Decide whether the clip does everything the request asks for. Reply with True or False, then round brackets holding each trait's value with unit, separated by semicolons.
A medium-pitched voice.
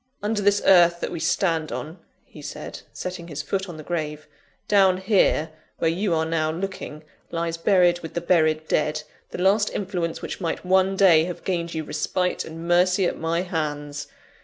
True (170 Hz)